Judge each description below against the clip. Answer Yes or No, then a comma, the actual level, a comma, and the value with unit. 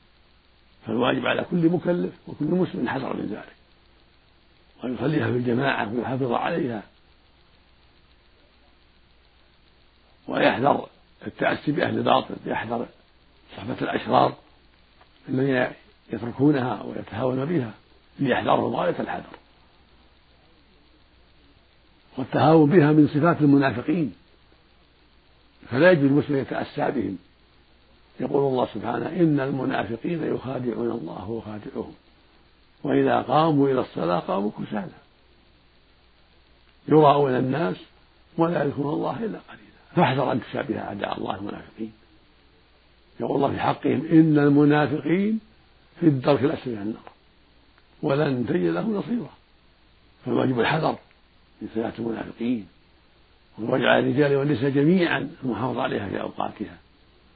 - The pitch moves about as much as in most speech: No, wide, 6.1 semitones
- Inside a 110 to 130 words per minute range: No, average, 100 wpm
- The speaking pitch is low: Yes, low, 130 Hz